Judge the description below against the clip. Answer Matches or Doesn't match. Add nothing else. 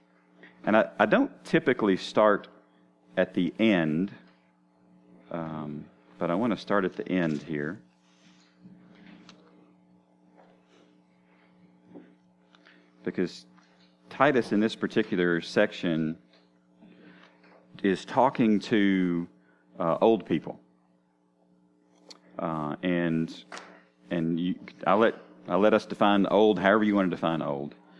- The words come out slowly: Matches